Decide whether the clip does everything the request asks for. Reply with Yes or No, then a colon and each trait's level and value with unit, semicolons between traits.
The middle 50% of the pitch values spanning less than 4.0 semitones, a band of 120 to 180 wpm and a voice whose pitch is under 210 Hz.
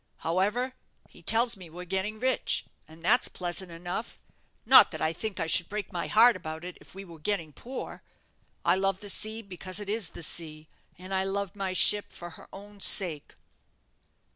No: average, 3.3 semitones; average, 190 wpm; high, 190 Hz